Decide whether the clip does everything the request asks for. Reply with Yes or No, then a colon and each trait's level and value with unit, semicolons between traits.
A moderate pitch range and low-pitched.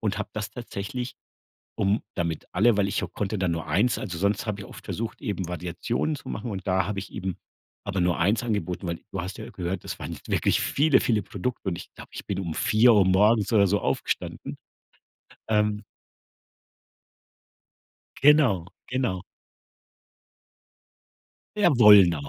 Yes: average, 3.2 semitones; low, 100 Hz